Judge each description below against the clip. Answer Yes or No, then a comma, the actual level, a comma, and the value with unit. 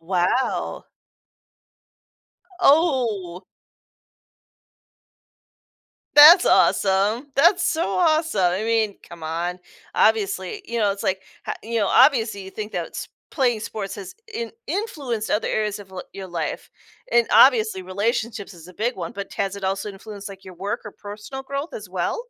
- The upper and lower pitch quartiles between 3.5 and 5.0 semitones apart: Yes, average, 4.3 semitones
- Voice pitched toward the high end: Yes, high, 210 Hz